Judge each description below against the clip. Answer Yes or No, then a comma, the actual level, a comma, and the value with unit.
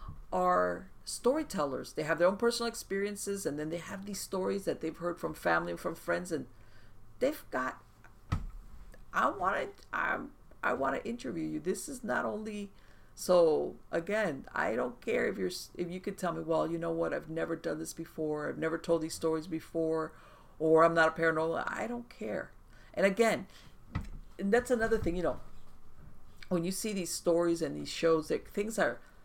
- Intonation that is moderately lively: Yes, average, 4.1 semitones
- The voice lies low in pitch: No, medium, 165 Hz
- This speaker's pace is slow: No, average, 190 wpm